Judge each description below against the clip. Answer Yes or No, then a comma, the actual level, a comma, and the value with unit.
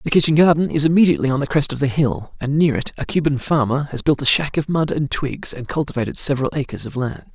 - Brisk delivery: Yes, fast, 255 wpm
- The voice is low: No, medium, 145 Hz